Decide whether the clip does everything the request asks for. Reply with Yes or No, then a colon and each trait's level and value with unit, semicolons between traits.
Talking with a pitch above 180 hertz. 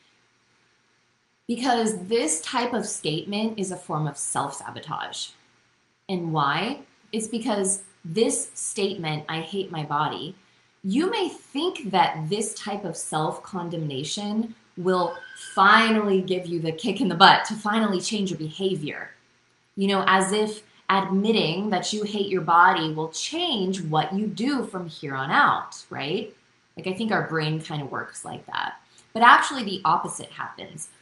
Yes: high, 190 Hz